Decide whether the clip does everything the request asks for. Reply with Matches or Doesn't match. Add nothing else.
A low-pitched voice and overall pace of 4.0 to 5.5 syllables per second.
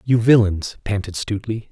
Matches